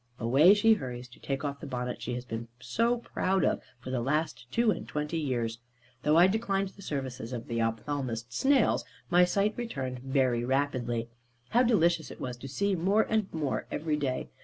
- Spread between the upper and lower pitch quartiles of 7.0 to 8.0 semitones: Yes, wide, 7.4 semitones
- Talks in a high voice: No, medium, 140 Hz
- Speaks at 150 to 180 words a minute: No, average, 190 wpm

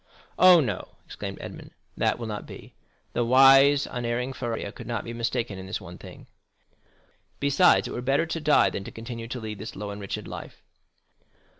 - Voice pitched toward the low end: Yes, low, 120 Hz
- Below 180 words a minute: No, average, 185 wpm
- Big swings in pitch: No, average, 3.9 semitones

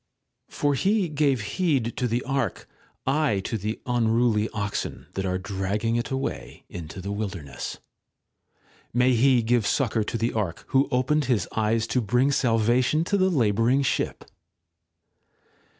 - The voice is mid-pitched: No, low, 120 Hz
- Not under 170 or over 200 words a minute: No, average, 145 wpm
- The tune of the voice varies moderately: Yes, average, 4.1 semitones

